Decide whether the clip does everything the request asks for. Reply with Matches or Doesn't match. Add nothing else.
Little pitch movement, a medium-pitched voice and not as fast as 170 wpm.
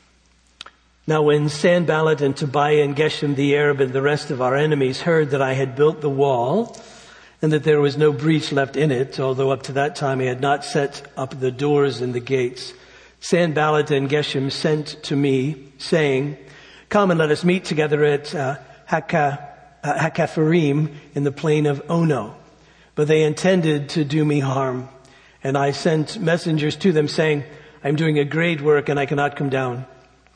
Doesn't match